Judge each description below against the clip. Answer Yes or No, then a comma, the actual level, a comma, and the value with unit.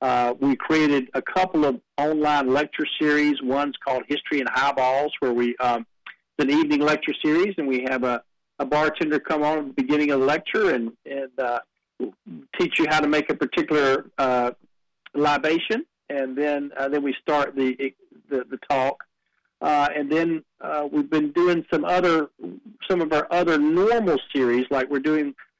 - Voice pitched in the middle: Yes, medium, 145 Hz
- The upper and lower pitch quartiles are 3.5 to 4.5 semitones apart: No, narrow, 2.6 semitones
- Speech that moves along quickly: No, average, 180 wpm